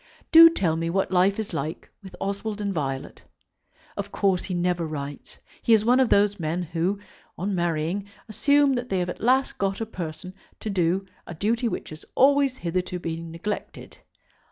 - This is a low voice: No, high, 190 Hz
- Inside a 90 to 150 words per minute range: No, average, 180 wpm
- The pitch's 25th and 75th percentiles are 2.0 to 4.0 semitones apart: No, average, 4.5 semitones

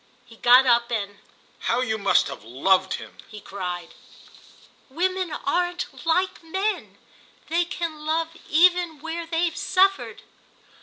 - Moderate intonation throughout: No, wide, 7.8 semitones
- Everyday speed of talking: No, slow, 125 wpm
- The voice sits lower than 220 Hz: No, very high, 315 Hz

